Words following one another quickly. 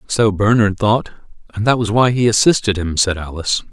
No: average, 195 wpm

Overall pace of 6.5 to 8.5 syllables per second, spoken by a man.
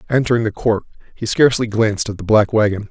Yes: 6.6 syllables/s; male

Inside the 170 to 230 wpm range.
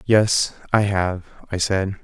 No: average, 145 wpm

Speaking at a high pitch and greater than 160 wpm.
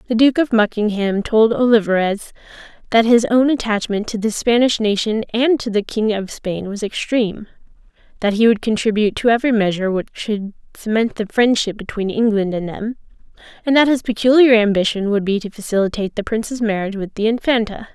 Yes: high, 220 Hz; average, 175 wpm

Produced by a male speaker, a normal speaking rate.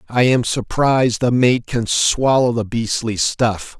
Yes: male; average, 160 wpm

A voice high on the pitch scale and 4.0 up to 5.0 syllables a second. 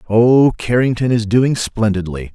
No: low, 115 Hz; 4.2 syllables/s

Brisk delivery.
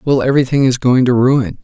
Yes: fast, 220 wpm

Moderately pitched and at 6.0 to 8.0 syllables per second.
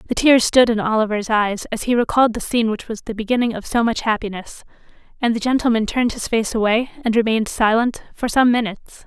No: high, 225 Hz; 6.2 syllables/s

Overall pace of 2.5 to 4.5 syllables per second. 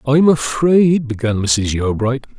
Yes: 4.2 syllables/s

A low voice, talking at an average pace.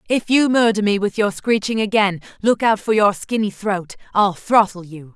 No: high, 205 Hz; average, 185 wpm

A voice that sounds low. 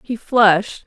No: high, 215 Hz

